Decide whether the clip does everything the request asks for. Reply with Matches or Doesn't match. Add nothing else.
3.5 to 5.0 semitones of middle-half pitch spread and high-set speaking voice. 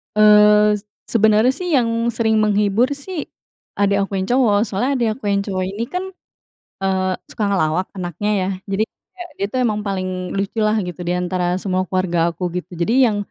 Doesn't match